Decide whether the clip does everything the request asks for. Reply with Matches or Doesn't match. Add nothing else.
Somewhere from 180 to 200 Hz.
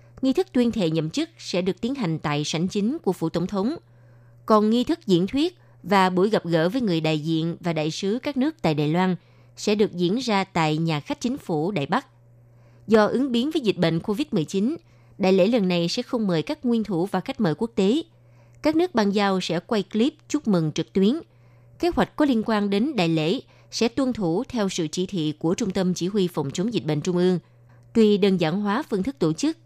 Matches